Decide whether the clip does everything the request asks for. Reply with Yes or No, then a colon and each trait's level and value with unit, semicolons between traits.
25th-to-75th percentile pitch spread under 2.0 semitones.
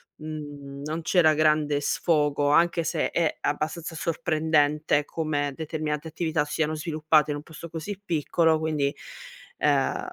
Yes: narrow, 1.5 semitones